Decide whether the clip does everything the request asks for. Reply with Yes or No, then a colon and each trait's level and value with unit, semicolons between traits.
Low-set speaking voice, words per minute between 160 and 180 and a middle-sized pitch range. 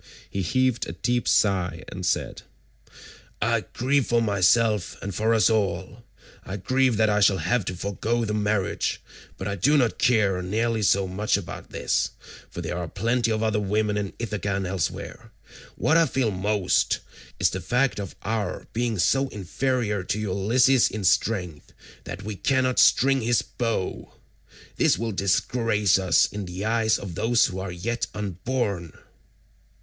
Yes: low, 105 Hz; average, 165 wpm; average, 3.5 semitones